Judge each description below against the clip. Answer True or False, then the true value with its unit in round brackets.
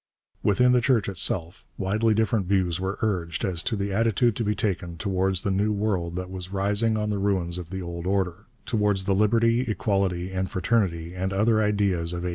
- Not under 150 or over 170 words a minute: False (200 wpm)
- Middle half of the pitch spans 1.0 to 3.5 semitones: True (2.8 semitones)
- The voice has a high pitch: False (95 Hz)